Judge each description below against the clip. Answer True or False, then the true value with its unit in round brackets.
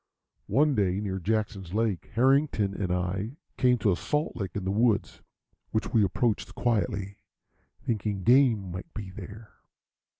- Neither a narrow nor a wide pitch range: True (3.5 semitones)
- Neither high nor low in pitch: False (105 Hz)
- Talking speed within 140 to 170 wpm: True (145 wpm)